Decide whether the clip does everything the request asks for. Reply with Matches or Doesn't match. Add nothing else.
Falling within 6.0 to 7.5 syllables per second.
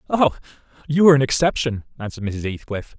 Matches